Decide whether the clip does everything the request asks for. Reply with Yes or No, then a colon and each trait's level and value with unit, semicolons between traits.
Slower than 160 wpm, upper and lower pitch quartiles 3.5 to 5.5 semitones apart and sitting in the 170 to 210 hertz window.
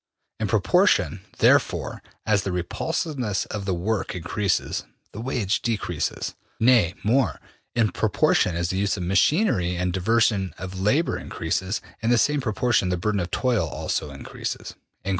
No: average, 145 wpm; average, 4.4 semitones; low, 100 Hz